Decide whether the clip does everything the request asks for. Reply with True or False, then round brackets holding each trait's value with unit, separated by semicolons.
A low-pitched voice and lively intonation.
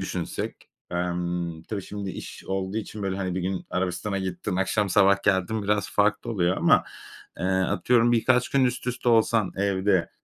False (100 Hz; 2.5 semitones)